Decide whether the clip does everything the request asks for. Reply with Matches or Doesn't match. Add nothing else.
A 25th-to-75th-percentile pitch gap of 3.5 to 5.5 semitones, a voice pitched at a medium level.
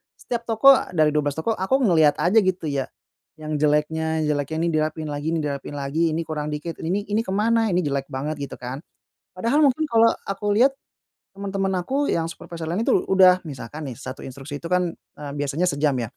Matches